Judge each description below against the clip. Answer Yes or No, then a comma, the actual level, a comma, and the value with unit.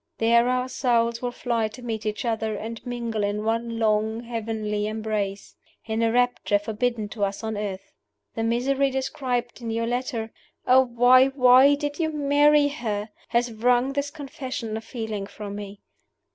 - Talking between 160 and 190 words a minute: Yes, average, 165 wpm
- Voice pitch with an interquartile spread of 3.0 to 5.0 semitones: No, narrow, 2.6 semitones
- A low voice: No, high, 230 Hz